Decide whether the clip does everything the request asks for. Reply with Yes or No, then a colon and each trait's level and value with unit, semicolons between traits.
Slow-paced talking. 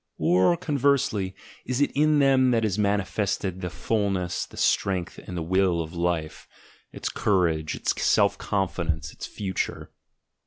No: average, 145 wpm